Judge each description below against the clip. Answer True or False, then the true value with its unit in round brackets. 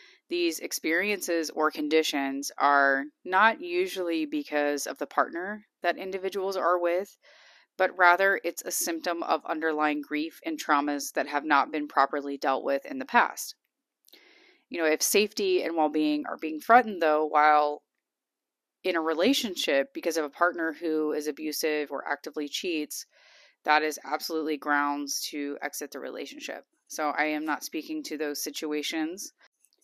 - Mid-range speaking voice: True (160 Hz)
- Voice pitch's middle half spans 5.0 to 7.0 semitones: False (4.3 semitones)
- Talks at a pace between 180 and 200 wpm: False (155 wpm)